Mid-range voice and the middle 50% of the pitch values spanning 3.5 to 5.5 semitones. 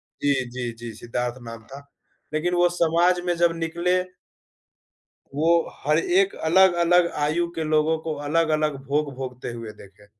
Yes: medium, 155 Hz; average, 5.1 semitones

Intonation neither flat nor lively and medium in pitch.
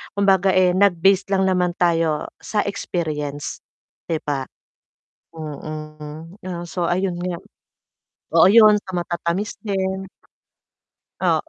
Yes: average, 3.2 semitones; medium, 175 Hz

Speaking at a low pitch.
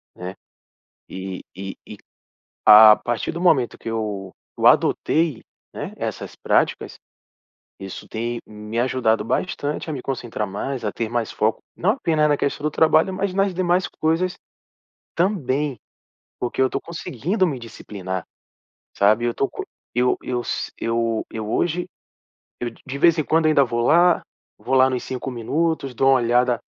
Yes: low, 130 Hz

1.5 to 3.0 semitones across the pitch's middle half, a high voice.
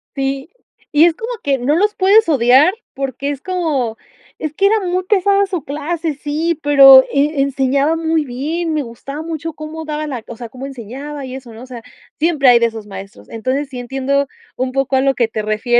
No: average, 3.9 semitones; very high, 280 Hz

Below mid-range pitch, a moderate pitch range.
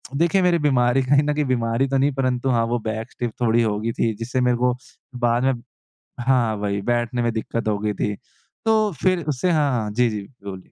Yes: low, 120 Hz; average, 3.2 semitones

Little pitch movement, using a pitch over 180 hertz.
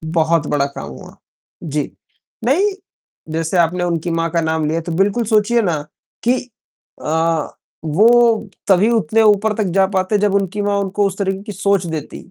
No: average, 4.2 semitones; high, 190 Hz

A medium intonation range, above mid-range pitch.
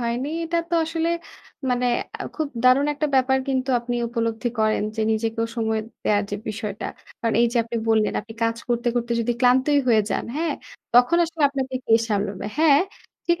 Yes: average, 3.7 semitones; high, 240 Hz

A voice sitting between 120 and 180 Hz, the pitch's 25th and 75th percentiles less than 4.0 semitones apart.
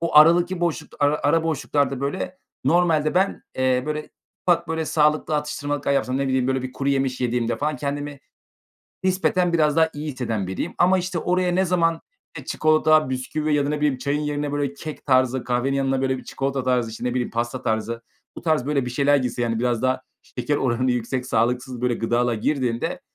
Yes: medium, 140 Hz; average, 3.4 semitones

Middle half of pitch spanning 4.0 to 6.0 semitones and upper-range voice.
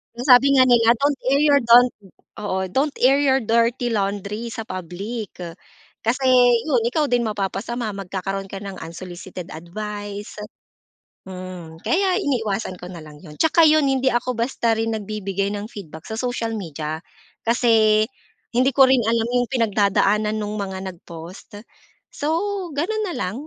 Yes: average, 4.3 semitones; high, 220 Hz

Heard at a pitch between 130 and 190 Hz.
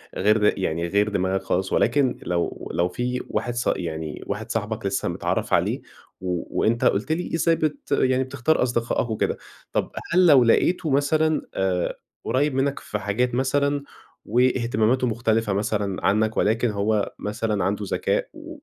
No: low, 115 Hz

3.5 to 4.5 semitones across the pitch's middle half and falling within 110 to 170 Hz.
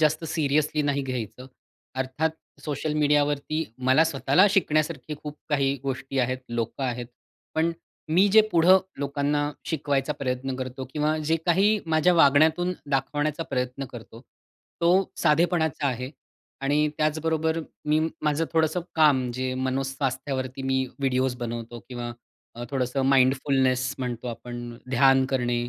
No: average, 3.1 semitones; medium, 140 Hz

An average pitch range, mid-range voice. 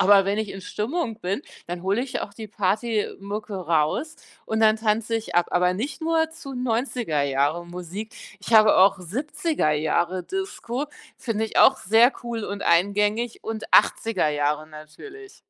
No: average, 4.7 semitones; high, 210 Hz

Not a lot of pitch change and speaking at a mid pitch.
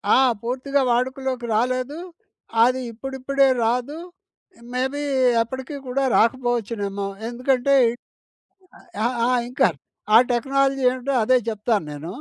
No: narrow, 2.3 semitones; very high, 255 Hz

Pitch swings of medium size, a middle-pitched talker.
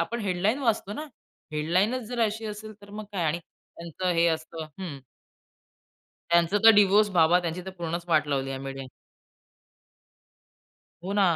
Yes: average, 4.3 semitones; medium, 180 Hz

